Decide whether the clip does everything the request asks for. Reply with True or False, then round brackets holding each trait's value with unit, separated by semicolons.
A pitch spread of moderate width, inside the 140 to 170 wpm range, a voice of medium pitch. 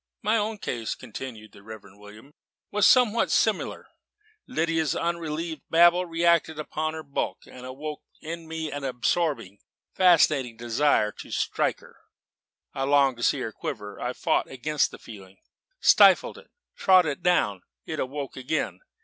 False (5.7 semitones; 150 wpm; 145 Hz)